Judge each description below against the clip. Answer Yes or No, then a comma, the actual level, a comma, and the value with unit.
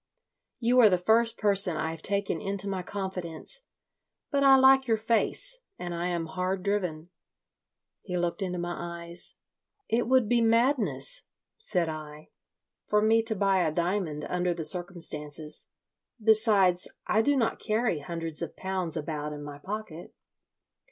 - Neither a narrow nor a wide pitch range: Yes, average, 4.6 semitones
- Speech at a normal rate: Yes, average, 150 wpm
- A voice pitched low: No, medium, 185 Hz